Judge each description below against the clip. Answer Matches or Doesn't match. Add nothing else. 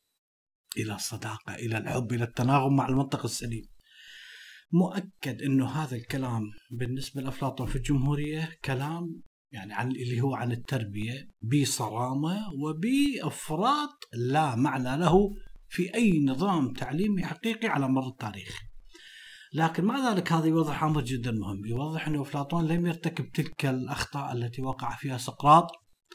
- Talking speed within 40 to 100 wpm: Doesn't match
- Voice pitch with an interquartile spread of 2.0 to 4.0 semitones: Doesn't match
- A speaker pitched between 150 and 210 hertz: Doesn't match